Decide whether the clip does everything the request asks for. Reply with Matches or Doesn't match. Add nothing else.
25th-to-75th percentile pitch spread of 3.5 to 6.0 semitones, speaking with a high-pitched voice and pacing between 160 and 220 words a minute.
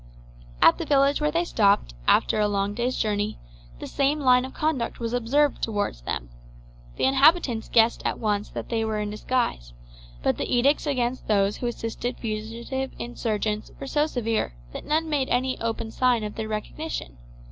Matches